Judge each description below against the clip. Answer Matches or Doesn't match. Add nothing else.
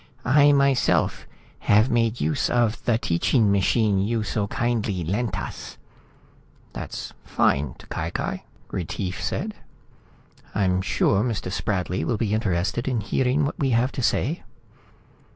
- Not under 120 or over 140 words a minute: Matches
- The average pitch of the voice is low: Matches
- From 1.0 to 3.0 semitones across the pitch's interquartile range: Doesn't match